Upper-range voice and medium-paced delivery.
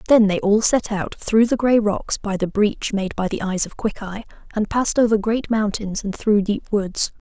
No: high, 210 Hz; fast, 225 wpm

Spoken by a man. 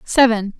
No: female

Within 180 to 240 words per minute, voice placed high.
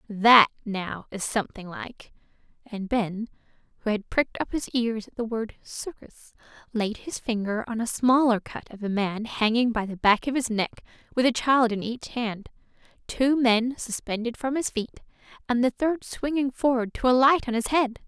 Yes: average, 185 wpm; high, 235 Hz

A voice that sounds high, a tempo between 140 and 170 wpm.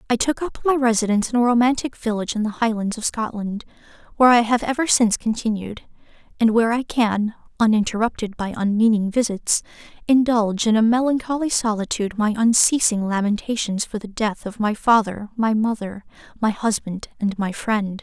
Yes: high, 220 Hz; average, 165 wpm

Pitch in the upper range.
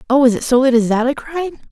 Yes: very high, 265 Hz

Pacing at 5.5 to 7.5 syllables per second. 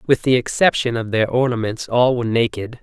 Yes: 5.6 syllables/s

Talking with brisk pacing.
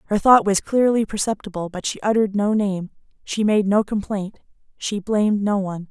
No: average, 185 wpm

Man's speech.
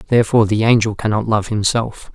Yes: male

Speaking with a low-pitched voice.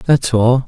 Yes: low, 125 Hz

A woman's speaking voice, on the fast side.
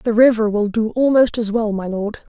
Yes: female; fast, 230 wpm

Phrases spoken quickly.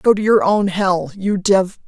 Yes: fast, 225 wpm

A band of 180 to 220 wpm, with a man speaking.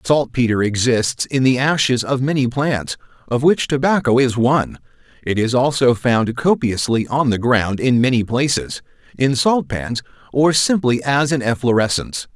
No: average, 150 wpm; male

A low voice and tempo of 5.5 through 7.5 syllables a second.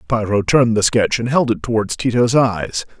No: low, 115 Hz; 5.1 syllables/s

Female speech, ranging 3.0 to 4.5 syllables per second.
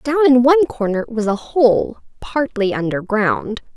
Yes: female; 4.2 syllables/s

